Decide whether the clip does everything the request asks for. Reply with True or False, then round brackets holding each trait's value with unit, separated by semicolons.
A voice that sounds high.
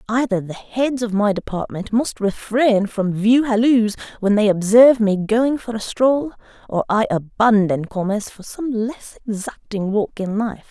True (220 Hz)